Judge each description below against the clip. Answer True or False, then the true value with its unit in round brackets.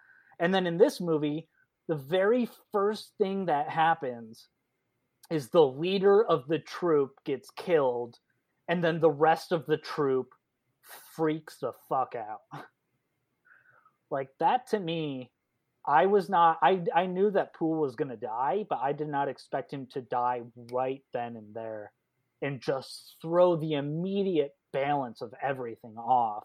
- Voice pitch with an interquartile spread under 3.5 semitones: False (5.2 semitones)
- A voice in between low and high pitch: True (155 Hz)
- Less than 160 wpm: True (150 wpm)